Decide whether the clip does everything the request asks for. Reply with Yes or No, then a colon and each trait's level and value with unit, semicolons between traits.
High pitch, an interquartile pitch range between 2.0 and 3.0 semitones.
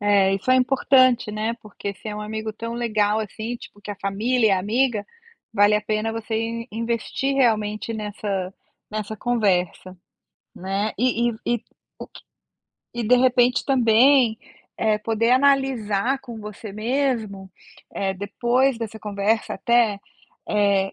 Yes: high, 220 Hz; narrow, 2.6 semitones